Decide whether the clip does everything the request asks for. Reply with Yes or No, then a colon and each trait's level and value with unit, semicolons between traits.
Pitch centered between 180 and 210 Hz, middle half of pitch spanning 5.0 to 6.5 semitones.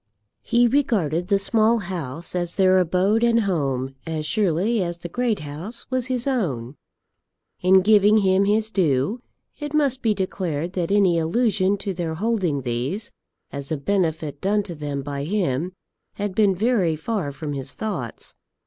Yes: medium, 185 Hz; wide, 5.5 semitones